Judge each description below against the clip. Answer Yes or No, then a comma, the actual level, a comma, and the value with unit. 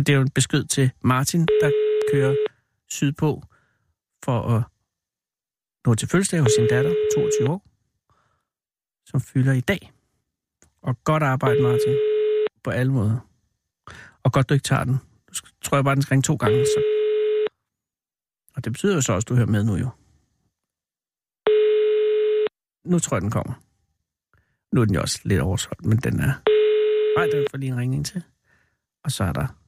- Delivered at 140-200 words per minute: Yes, average, 170 wpm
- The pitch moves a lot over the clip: Yes, wide, 6.1 semitones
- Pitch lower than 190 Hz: Yes, medium, 140 Hz